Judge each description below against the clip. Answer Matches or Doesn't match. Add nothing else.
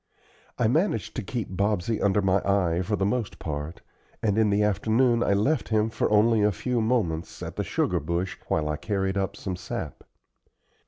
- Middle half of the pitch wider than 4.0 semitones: Doesn't match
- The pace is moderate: Matches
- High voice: Doesn't match